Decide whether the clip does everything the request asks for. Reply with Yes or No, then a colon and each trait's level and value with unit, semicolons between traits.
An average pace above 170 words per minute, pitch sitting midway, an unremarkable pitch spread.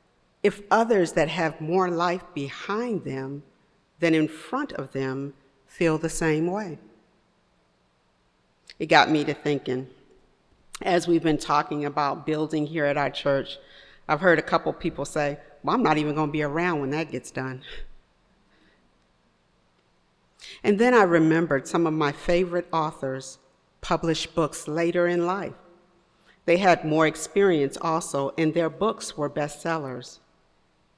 No: average, 140 wpm; medium, 155 Hz; average, 3.6 semitones